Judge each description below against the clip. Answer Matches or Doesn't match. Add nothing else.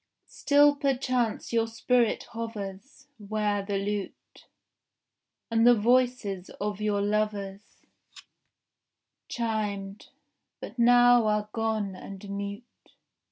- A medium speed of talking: Doesn't match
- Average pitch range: Matches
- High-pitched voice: Matches